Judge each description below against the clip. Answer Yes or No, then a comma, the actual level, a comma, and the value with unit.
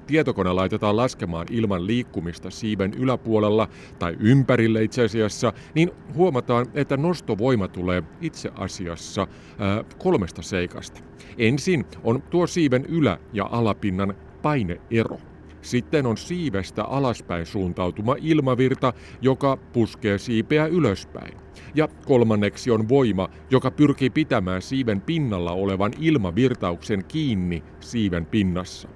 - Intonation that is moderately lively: No, wide, 6.1 semitones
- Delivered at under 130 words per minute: Yes, average, 110 wpm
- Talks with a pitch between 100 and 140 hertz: Yes, low, 110 Hz